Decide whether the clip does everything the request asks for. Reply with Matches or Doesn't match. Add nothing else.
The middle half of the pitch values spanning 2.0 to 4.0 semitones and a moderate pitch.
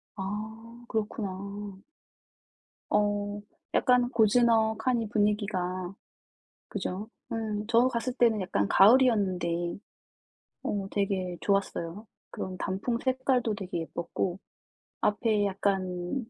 Doesn't match